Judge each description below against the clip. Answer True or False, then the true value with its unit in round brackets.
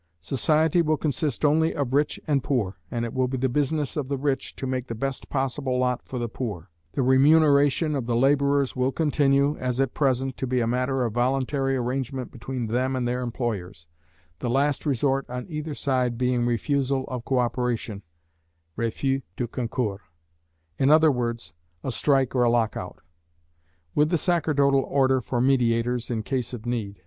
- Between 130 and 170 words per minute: False (180 wpm)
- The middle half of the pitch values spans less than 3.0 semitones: True (2.5 semitones)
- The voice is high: False (130 Hz)